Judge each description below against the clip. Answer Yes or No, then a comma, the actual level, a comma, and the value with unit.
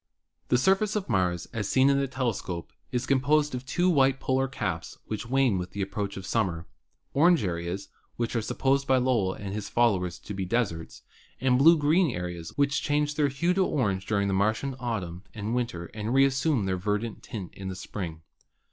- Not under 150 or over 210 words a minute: Yes, average, 200 wpm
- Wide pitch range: Yes, wide, 6.1 semitones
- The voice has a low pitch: Yes, low, 115 Hz